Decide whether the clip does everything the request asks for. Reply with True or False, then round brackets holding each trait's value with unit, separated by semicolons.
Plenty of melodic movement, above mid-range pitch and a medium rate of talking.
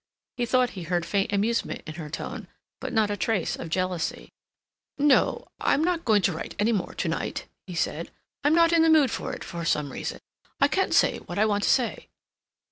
False (6.5 semitones; 205 Hz; 210 wpm)